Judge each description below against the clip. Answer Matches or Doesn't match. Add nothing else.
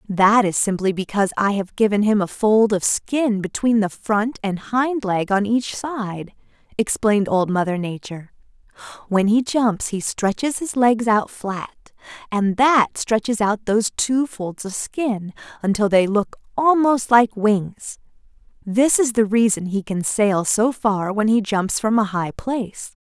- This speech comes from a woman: Matches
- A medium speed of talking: Matches